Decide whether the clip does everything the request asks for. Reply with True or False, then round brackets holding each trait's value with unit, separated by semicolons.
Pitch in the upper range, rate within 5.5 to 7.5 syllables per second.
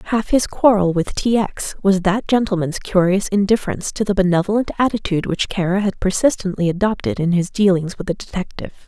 True (195 Hz; 6.0 syllables/s)